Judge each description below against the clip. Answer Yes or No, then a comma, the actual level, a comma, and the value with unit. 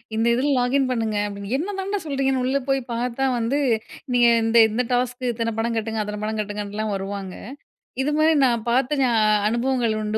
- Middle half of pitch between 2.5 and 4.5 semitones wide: Yes, average, 3.5 semitones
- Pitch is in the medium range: No, high, 235 Hz